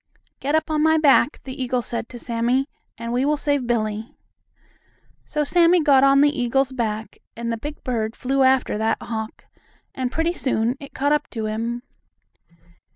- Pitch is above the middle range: Yes, very high, 255 Hz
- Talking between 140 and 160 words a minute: No, average, 175 wpm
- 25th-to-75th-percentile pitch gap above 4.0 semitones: No, average, 3.7 semitones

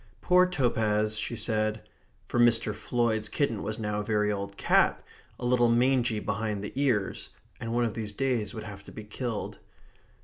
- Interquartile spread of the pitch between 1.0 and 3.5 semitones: Yes, narrow, 2.4 semitones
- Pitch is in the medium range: No, low, 110 Hz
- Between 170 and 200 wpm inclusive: Yes, average, 175 wpm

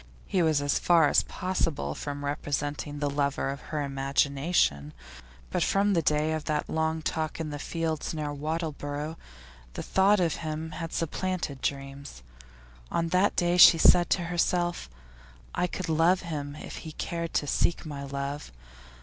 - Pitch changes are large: No, average, 2.8 semitones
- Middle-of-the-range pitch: Yes, medium, 155 Hz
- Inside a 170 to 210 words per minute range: No, average, 160 wpm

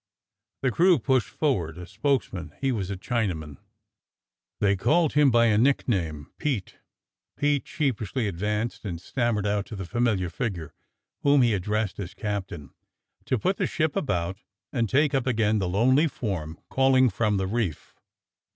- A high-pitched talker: No, low, 110 Hz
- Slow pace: No, average, 160 wpm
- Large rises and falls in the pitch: Yes, wide, 5.8 semitones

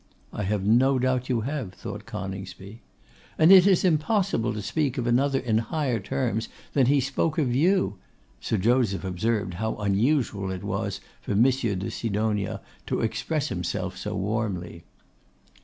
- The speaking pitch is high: No, low, 115 Hz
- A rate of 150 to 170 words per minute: Yes, average, 155 wpm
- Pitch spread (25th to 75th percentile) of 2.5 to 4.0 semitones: No, average, 5.1 semitones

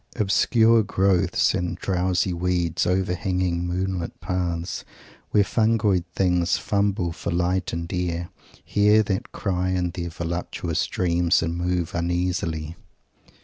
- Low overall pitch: Yes, very low, 90 Hz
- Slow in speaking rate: Yes, slow, 120 wpm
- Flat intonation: Yes, narrow, 1.7 semitones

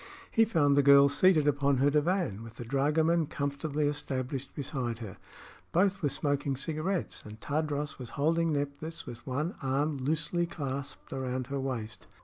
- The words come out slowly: No, average, 155 wpm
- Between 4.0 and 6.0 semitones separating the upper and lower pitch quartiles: No, average, 2.8 semitones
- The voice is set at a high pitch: No, medium, 140 Hz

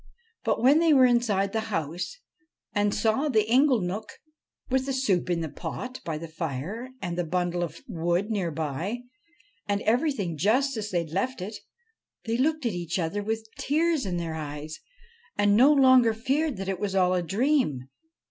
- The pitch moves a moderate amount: No, wide, 6.6 semitones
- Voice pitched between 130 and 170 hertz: No, high, 205 Hz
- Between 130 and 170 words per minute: No, average, 180 wpm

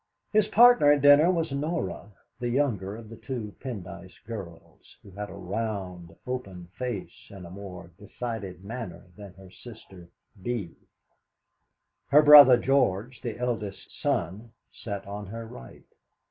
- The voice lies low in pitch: Yes, low, 110 Hz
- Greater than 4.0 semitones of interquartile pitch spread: Yes, average, 4.9 semitones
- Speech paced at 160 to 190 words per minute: No, average, 140 wpm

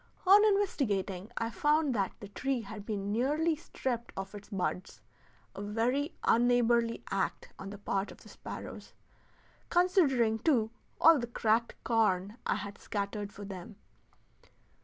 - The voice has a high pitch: Yes, high, 225 Hz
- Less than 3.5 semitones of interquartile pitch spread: No, average, 4.9 semitones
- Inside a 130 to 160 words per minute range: Yes, average, 140 wpm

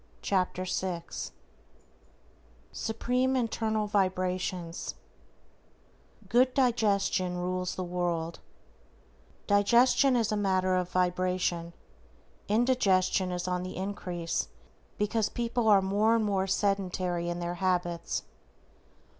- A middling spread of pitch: Yes, average, 3.1 semitones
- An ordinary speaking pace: No, slow, 95 wpm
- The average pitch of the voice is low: No, medium, 185 Hz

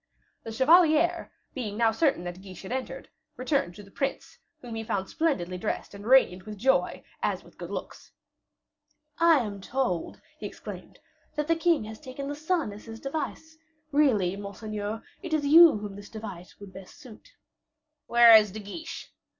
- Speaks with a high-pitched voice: Yes, high, 225 Hz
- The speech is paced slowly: No, average, 175 wpm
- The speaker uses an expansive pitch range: Yes, wide, 6.7 semitones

